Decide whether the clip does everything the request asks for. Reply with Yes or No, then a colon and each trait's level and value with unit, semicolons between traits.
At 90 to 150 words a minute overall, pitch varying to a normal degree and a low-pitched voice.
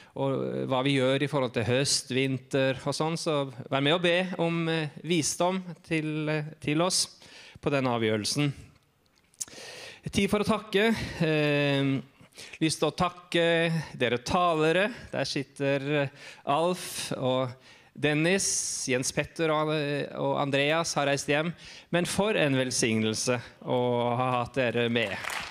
No: slow, 135 wpm; average, 4.1 semitones; medium, 145 Hz